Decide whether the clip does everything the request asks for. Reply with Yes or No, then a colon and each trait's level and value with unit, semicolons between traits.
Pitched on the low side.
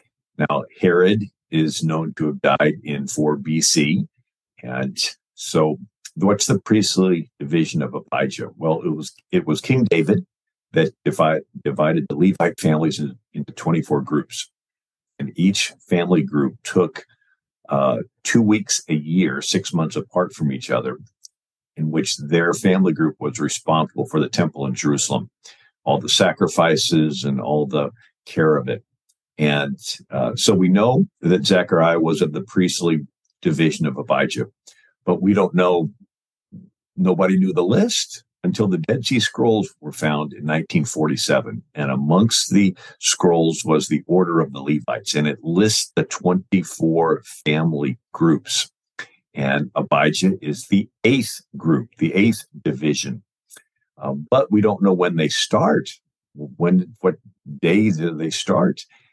Yes: very low, 80 Hz